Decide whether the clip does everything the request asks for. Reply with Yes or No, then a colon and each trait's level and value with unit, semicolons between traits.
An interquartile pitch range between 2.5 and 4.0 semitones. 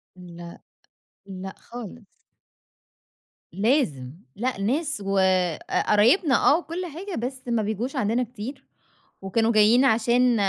No: average, 4.7 semitones